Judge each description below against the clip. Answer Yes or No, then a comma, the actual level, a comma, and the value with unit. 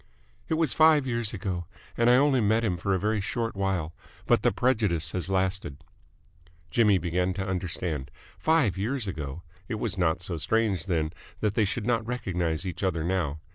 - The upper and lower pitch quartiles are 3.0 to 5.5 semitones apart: Yes, average, 4.7 semitones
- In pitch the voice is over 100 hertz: No, very low, 95 Hz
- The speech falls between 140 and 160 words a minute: No, average, 180 wpm